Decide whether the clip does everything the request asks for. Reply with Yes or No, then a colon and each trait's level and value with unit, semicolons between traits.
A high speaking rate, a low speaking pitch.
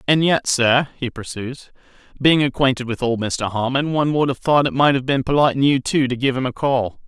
Yes: fast, 235 wpm; low, 130 Hz